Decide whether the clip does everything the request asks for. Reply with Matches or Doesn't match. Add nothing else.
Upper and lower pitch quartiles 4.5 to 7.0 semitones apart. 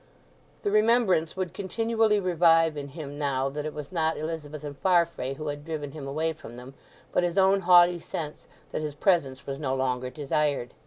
Doesn't match